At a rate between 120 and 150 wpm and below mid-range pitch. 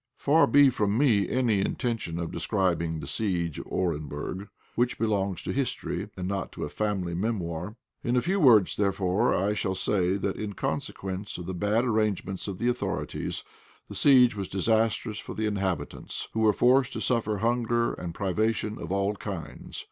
No: average, 175 wpm; low, 105 Hz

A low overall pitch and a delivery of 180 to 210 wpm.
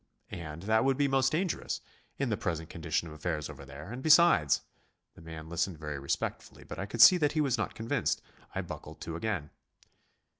Yes: very low, 95 Hz; average, 195 wpm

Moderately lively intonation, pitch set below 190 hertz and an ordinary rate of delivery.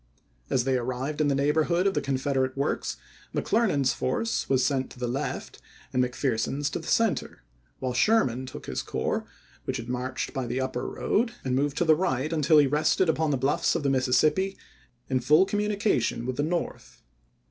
Yes: average, 3.7 semitones; medium, 140 Hz; average, 185 wpm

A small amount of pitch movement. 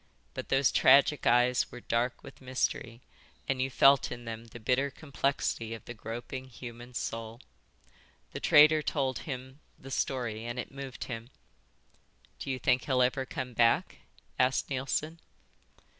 Yes: narrow, 2.2 semitones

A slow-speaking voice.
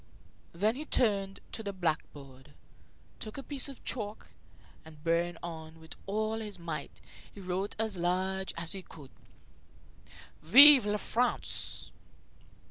Yes: slow, 130 wpm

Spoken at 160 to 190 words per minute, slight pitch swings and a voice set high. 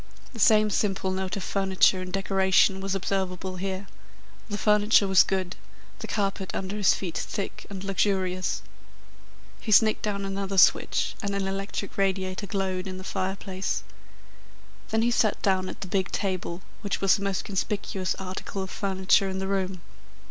Yes: average, 165 wpm; narrow, 1.1 semitones; high, 195 Hz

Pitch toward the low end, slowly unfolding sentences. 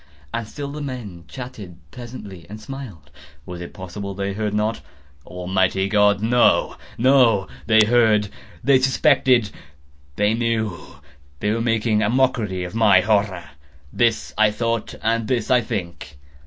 Yes: low, 105 Hz; slow, 125 wpm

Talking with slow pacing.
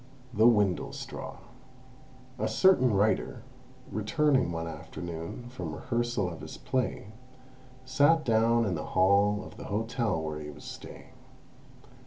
Yes: slow, 125 wpm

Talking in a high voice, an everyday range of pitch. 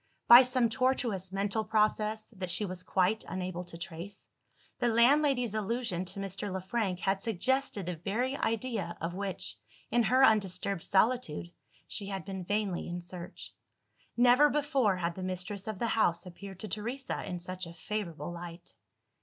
Yes: high, 200 Hz; average, 4.2 semitones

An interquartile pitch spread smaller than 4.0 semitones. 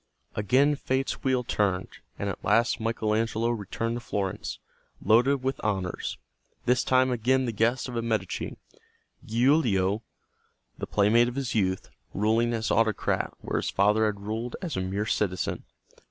Yes: average, 3.1 semitones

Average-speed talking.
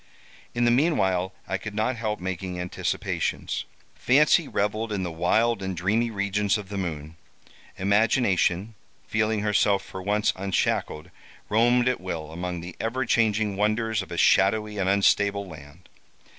Yes: average, 145 wpm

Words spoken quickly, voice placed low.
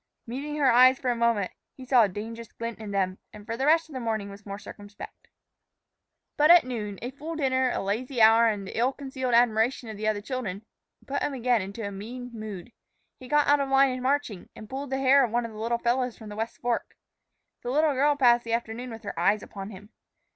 No: fast, 235 wpm; high, 235 Hz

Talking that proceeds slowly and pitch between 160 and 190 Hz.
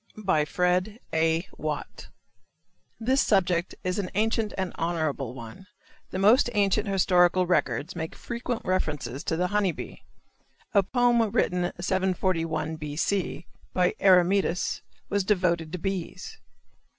Yes: slow, 125 wpm; medium, 185 Hz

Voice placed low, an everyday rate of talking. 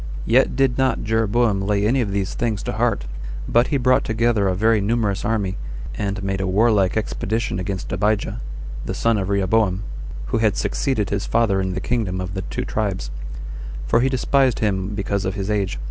Yes: low, 105 Hz; average, 190 wpm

